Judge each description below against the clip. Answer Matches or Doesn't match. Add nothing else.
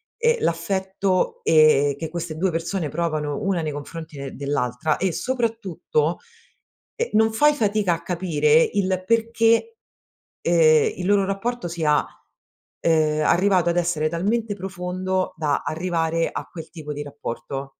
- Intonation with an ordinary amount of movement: Matches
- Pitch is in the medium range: Matches